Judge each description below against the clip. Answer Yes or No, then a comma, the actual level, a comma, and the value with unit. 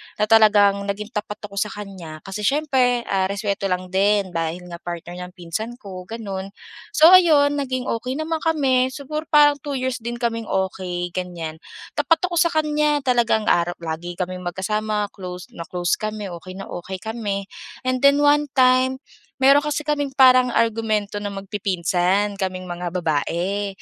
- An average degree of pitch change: No, wide, 5.9 semitones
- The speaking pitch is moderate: No, high, 210 Hz